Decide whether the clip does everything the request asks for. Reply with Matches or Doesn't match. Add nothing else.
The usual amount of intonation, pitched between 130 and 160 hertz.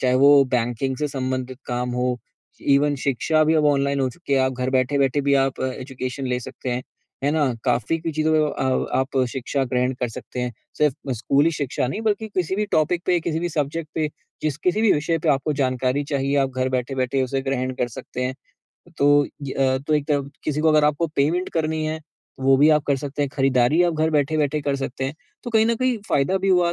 Matches